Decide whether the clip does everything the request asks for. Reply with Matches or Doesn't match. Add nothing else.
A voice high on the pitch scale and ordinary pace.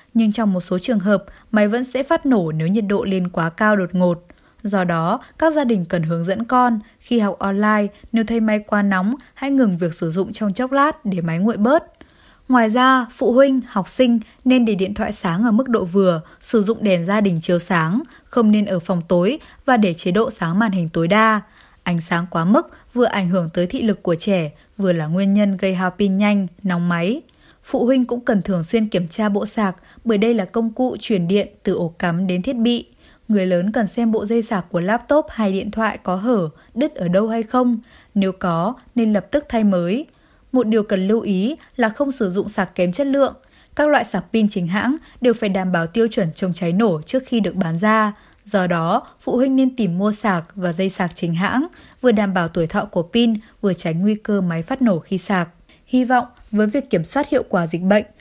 Matches